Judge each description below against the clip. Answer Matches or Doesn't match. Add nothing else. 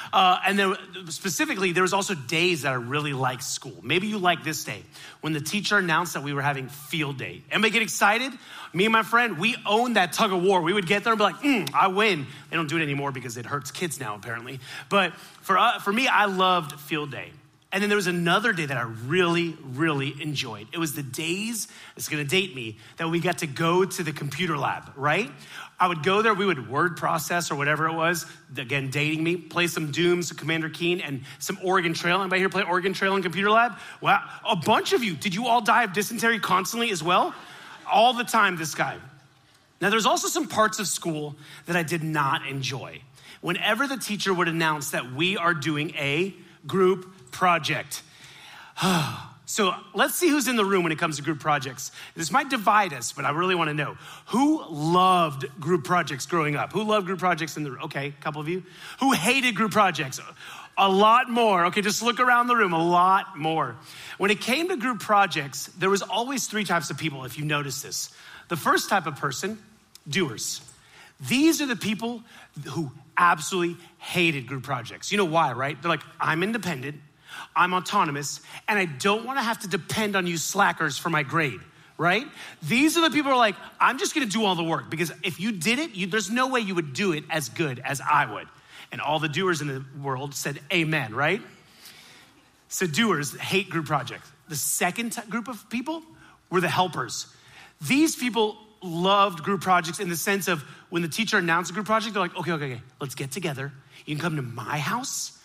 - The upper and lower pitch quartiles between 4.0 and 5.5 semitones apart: Matches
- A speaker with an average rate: Doesn't match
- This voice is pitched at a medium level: Matches